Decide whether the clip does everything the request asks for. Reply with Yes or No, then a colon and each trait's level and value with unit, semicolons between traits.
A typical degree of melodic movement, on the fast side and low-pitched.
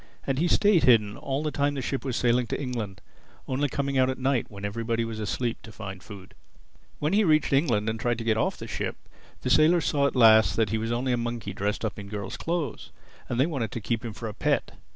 Yes: average, 4.0 semitones; fast, 240 wpm; low, 120 Hz